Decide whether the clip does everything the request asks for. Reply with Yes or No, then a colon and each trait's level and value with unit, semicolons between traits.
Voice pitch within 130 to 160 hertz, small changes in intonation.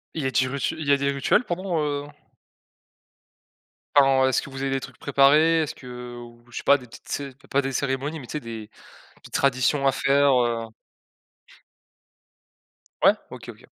Yes: low, 135 Hz; narrow, 2.0 semitones